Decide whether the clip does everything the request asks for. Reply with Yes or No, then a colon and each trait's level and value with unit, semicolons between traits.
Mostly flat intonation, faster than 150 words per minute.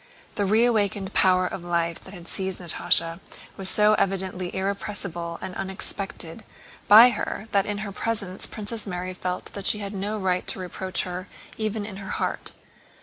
Yes: narrow, 2.2 semitones; average, 165 wpm